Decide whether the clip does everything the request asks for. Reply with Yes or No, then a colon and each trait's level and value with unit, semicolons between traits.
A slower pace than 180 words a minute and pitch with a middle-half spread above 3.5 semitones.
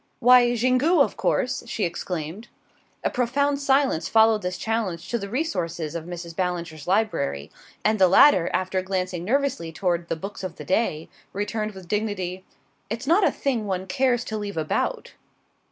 Yes: average, 165 wpm; wide, 5.4 semitones